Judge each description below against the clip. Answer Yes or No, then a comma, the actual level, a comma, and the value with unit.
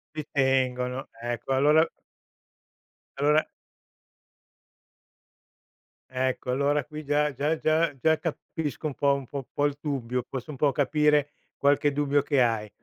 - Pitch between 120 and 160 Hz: Yes, medium, 140 Hz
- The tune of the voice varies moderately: No, narrow, 2.3 semitones